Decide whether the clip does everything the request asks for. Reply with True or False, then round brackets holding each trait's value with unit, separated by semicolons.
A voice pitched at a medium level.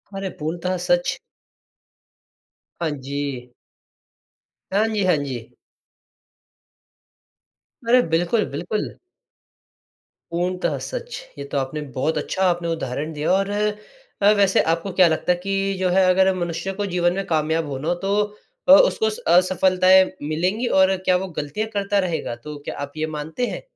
True (180 Hz)